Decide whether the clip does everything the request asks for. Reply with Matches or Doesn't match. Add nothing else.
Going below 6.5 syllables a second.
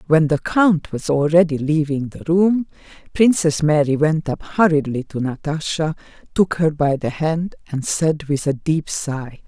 Matches